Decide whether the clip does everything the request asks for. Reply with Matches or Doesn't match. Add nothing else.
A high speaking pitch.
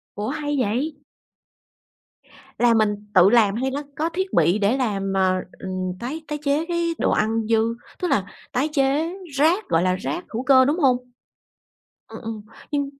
Matches